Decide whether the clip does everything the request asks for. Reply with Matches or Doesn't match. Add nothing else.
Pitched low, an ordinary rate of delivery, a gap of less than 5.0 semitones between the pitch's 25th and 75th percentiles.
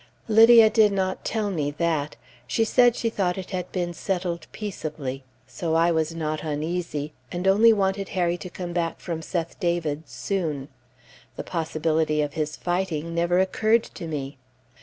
Doesn't match